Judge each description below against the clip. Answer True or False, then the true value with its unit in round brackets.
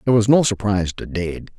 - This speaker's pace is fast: True (225 wpm)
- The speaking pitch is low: True (105 Hz)